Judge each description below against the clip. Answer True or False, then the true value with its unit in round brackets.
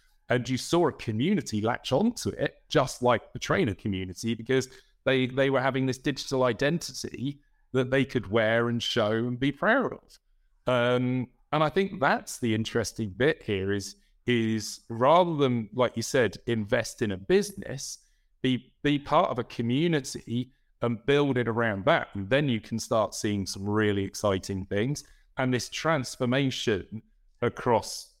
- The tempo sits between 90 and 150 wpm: False (160 wpm)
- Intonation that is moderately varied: True (3.6 semitones)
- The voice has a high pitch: False (125 Hz)